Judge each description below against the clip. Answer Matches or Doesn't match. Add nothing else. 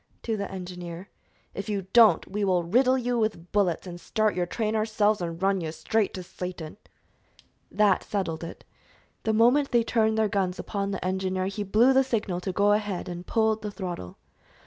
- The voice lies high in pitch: Matches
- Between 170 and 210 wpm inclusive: Matches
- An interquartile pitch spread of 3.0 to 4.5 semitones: Matches